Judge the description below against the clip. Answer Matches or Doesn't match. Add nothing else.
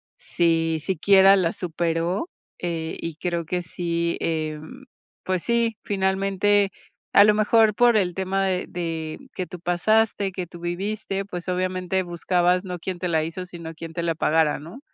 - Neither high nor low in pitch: Matches